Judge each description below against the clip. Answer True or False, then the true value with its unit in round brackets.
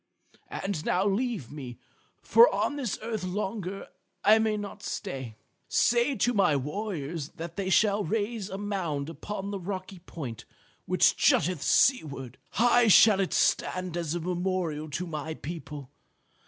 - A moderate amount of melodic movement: True (4.9 semitones)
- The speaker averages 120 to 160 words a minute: True (145 wpm)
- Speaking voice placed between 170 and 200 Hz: True (185 Hz)